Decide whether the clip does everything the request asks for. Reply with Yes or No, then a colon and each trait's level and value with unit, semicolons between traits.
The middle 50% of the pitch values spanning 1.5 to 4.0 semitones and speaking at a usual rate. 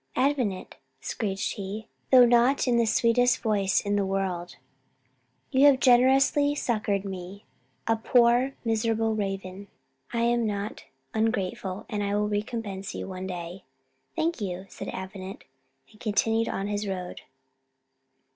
No: average, 3.5 semitones; slow, 130 wpm